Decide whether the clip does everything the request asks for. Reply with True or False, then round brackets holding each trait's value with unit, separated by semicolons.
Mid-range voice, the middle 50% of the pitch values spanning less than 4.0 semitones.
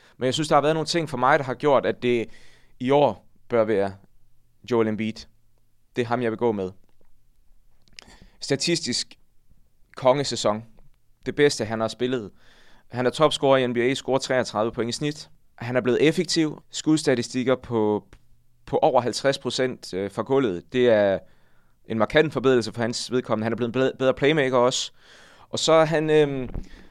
False (125 Hz; 3.3 semitones)